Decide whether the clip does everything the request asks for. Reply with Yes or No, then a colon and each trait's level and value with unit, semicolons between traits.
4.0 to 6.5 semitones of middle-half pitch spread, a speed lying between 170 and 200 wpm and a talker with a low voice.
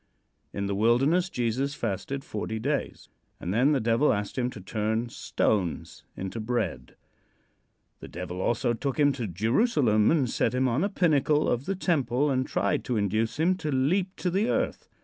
Yes: wide, 5.4 semitones; average, 175 wpm; low, 125 Hz